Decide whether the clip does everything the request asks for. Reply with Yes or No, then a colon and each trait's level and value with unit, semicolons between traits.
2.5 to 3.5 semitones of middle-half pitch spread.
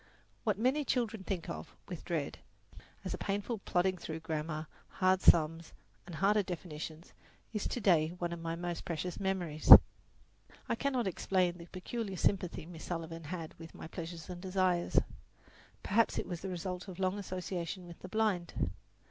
Yes: average, 2.8 semitones